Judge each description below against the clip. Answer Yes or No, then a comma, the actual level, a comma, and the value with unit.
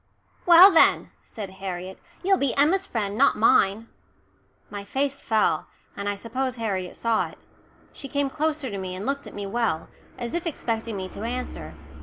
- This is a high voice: Yes, high, 230 Hz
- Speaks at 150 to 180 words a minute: Yes, average, 175 wpm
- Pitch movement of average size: No, wide, 5.8 semitones